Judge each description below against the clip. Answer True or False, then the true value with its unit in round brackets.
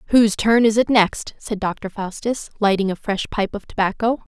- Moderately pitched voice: False (210 Hz)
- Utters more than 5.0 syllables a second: True (5.2 syllables/s)